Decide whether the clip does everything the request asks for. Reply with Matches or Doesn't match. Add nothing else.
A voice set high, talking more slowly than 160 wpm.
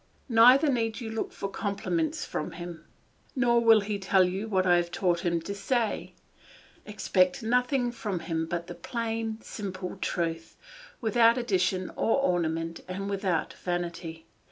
Matches